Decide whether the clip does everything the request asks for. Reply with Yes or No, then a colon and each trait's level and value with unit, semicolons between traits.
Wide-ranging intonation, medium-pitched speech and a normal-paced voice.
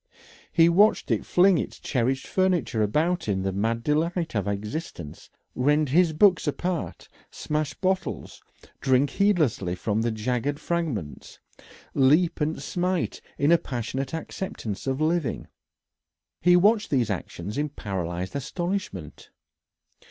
No: wide, 7.5 semitones; medium, 145 Hz; slow, 125 wpm